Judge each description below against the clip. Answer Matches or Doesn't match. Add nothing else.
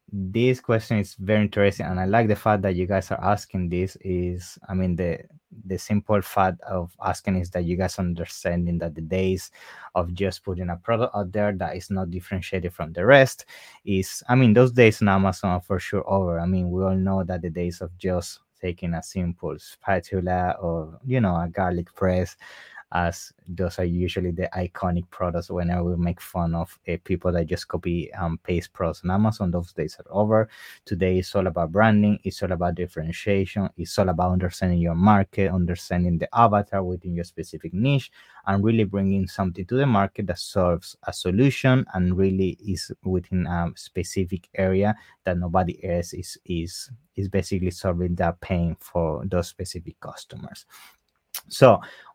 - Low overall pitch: Matches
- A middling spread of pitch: Doesn't match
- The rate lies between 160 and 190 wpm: Matches